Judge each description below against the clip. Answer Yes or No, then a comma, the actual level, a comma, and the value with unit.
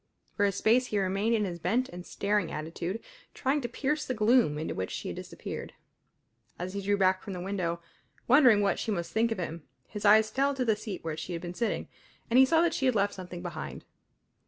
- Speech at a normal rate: No, fast, 230 wpm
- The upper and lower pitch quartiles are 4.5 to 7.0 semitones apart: Yes, average, 4.8 semitones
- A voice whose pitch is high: Yes, high, 205 Hz